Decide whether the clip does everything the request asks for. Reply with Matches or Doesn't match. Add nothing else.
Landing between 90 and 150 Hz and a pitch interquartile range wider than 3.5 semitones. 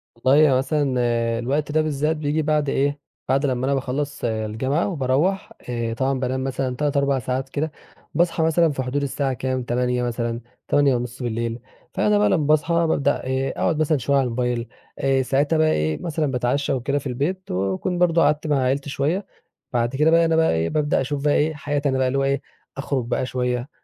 Doesn't match